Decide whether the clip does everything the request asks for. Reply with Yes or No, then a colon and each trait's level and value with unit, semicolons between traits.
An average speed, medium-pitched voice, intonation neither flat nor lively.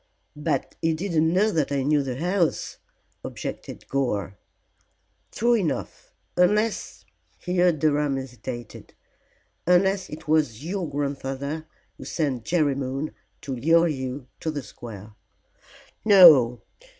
No: slow, 115 wpm; medium, 150 Hz; average, 4.7 semitones